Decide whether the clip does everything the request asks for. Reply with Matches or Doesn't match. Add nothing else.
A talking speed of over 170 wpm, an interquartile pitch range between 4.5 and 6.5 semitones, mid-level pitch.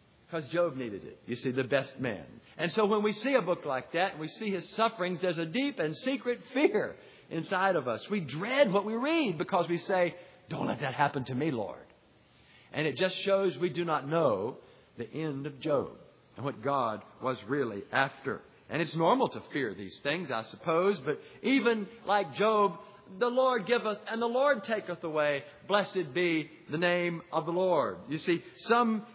Matches